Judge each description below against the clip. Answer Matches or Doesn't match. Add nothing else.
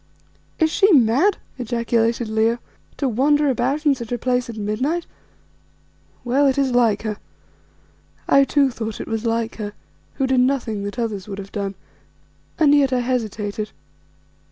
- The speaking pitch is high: Matches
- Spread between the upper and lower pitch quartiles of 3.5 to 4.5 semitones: Matches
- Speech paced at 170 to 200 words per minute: Doesn't match